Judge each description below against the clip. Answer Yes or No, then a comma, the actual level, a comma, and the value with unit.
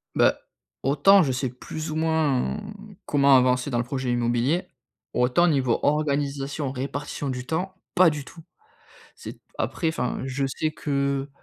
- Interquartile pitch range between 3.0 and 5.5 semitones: Yes, average, 3.3 semitones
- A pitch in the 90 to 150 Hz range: Yes, medium, 140 Hz